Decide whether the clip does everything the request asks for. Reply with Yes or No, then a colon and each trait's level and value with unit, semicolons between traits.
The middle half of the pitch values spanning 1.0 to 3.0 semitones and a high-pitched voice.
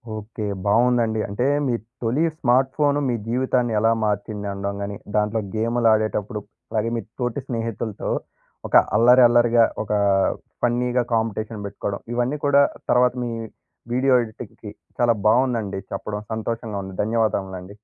No: narrow, 2.6 semitones; low, 115 Hz